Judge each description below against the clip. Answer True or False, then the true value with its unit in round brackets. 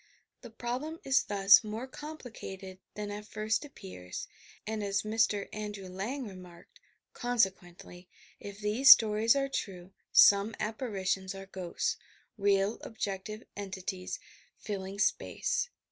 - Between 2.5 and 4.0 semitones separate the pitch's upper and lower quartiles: True (2.9 semitones)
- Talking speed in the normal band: False (125 wpm)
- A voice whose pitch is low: False (205 Hz)